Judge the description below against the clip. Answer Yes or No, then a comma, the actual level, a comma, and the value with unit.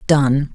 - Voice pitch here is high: No, medium, 140 Hz